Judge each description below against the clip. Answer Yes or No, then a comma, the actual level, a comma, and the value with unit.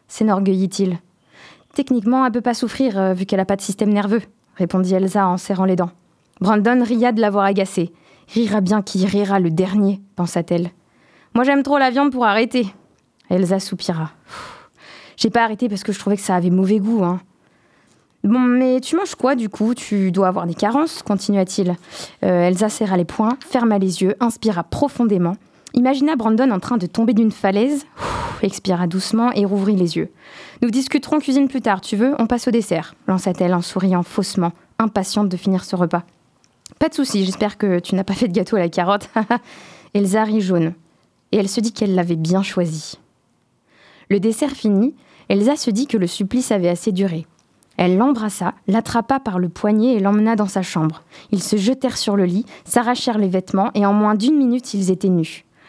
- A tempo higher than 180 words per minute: Yes, average, 190 wpm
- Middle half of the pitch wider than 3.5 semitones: Yes, average, 4.1 semitones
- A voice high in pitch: Yes, high, 205 Hz